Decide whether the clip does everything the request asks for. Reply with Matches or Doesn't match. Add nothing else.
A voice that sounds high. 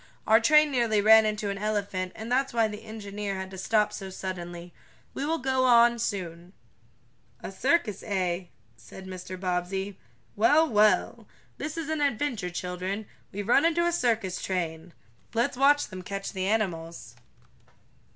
Matches